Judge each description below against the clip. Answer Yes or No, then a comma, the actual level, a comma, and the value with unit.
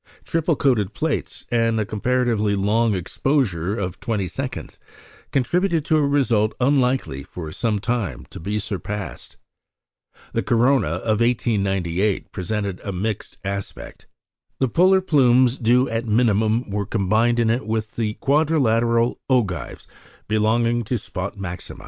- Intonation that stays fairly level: No, average, 3.8 semitones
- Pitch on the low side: Yes, low, 110 Hz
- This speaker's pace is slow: Yes, slow, 130 wpm